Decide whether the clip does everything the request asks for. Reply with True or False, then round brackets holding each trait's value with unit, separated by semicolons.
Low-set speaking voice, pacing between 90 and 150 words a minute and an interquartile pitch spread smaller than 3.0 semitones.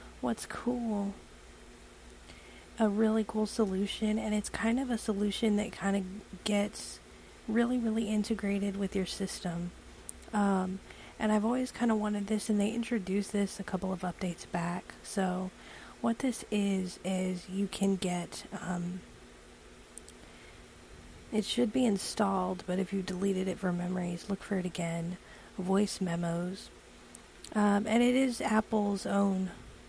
False (200 Hz; 145 wpm; 2.6 semitones)